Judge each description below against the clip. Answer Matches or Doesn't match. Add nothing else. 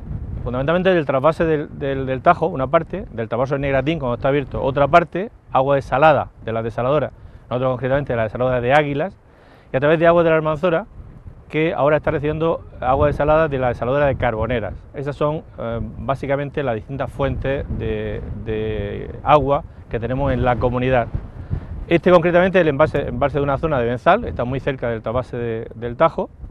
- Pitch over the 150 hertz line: Doesn't match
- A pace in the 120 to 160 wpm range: Doesn't match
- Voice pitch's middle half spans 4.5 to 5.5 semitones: Matches